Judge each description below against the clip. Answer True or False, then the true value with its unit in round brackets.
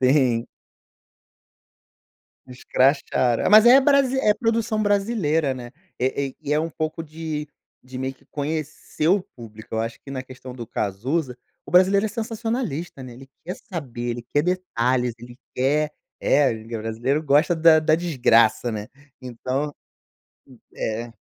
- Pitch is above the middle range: False (145 Hz)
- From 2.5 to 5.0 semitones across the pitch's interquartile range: False (5.5 semitones)